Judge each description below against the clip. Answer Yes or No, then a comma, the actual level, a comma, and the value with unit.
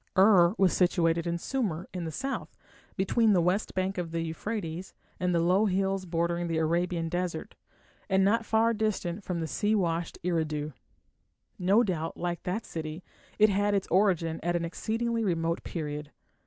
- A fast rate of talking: No, average, 165 wpm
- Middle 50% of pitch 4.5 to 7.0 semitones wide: No, average, 3.3 semitones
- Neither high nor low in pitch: Yes, medium, 180 Hz